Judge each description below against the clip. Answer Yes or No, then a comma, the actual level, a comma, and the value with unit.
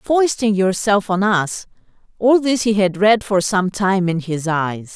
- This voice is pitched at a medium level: No, high, 200 Hz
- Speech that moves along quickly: No, average, 180 wpm